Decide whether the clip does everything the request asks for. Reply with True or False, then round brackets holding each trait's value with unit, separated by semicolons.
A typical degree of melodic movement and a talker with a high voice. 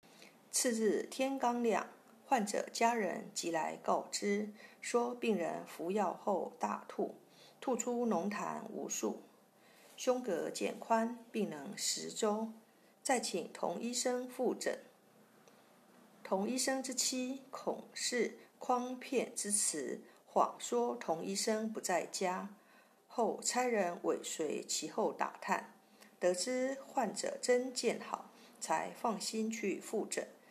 True (3.0 semitones; 235 Hz)